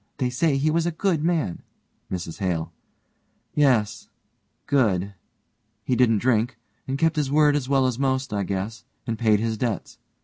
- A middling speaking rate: Yes, average, 165 wpm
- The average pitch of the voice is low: Yes, low, 125 Hz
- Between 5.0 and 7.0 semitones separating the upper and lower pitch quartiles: Yes, average, 5.3 semitones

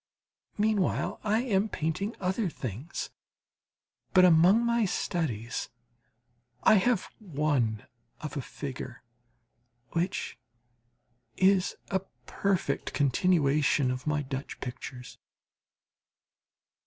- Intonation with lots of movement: Yes, wide, 6.5 semitones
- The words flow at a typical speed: No, slow, 90 wpm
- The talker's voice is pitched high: No, medium, 165 Hz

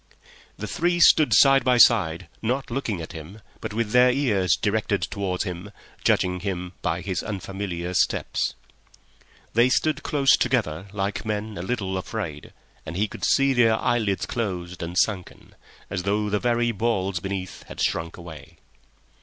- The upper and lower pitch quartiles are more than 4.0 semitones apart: Yes, average, 4.5 semitones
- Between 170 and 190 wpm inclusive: No, average, 155 wpm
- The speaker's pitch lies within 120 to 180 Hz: No, low, 100 Hz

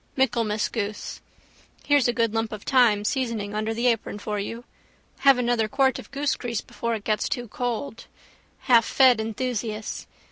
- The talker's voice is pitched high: Yes, high, 230 Hz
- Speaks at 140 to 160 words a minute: Yes, average, 150 wpm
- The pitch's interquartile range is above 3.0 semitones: No, narrow, 2.6 semitones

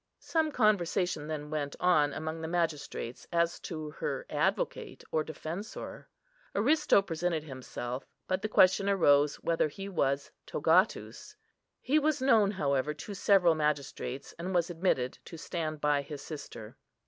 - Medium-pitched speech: Yes, medium, 165 Hz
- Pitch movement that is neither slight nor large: Yes, average, 4.7 semitones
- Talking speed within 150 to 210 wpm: No, average, 140 wpm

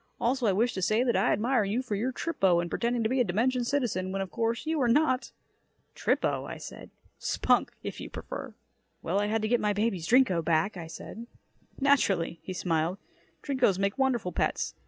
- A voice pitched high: Yes, high, 220 Hz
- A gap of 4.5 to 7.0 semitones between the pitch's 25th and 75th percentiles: Yes, average, 5.0 semitones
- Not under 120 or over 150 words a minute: No, average, 195 wpm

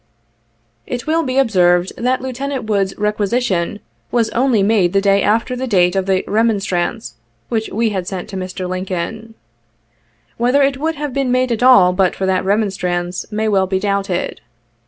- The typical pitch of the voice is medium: No, high, 210 Hz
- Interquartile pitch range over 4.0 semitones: Yes, average, 4.6 semitones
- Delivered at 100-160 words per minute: No, average, 175 wpm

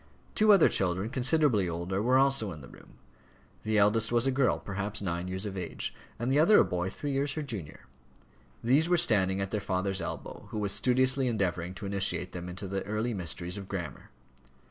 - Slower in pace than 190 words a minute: No, average, 200 wpm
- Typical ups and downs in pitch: No, wide, 5.7 semitones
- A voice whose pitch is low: Yes, low, 100 Hz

